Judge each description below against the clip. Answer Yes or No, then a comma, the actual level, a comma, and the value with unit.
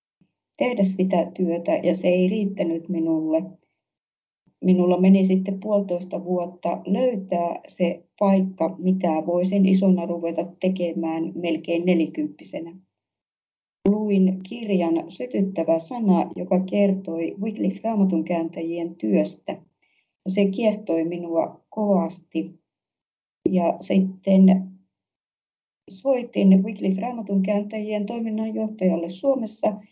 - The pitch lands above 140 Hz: Yes, medium, 185 Hz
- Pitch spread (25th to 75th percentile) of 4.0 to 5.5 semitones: No, average, 2.7 semitones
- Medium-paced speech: No, slow, 90 wpm